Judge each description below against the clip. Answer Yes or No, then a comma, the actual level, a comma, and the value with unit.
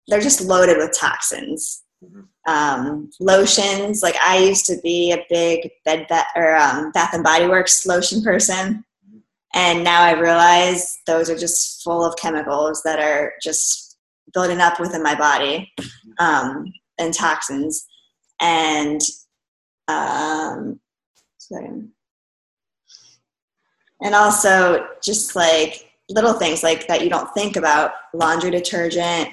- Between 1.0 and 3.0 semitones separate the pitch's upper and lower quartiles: Yes, narrow, 2.6 semitones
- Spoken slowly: Yes, slow, 125 wpm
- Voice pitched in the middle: Yes, medium, 170 Hz